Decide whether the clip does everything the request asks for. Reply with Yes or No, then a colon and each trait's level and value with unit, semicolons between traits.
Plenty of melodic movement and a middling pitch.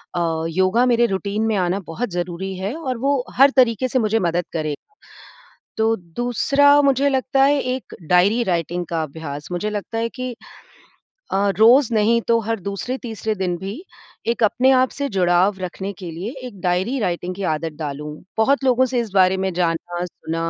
No: wide, 5.7 semitones; high, 205 Hz